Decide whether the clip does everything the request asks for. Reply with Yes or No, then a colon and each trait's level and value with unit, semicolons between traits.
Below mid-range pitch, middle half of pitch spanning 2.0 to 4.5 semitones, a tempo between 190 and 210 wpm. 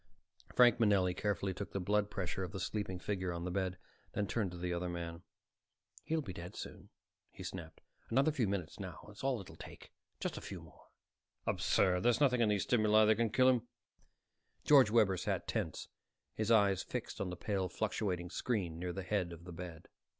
Yes: low, 100 Hz; average, 3.4 semitones; average, 195 wpm